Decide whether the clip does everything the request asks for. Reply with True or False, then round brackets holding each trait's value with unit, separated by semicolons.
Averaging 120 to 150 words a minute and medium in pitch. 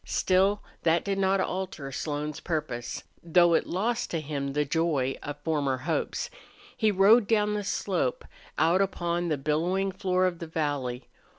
False (160 wpm; 170 Hz)